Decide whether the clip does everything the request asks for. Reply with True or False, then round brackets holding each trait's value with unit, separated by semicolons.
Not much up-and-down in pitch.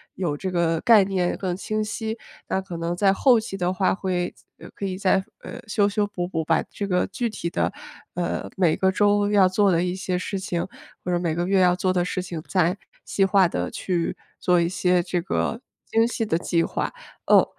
True (2.3 semitones)